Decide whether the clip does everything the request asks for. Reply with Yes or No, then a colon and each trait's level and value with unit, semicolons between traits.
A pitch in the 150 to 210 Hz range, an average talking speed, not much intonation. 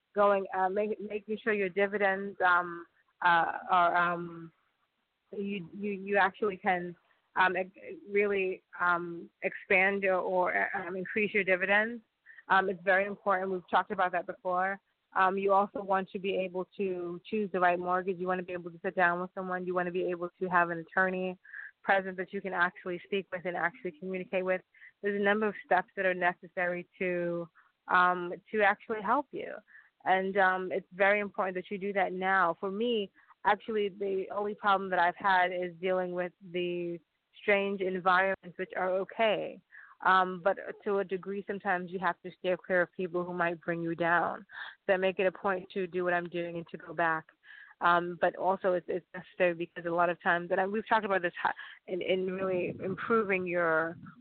Yes: medium, 185 Hz; average, 190 wpm; narrow, 1.8 semitones